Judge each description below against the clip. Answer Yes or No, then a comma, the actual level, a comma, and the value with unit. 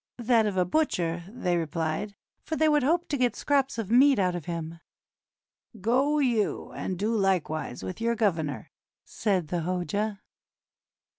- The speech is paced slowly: No, average, 165 wpm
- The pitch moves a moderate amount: No, wide, 6.0 semitones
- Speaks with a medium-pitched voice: No, high, 205 Hz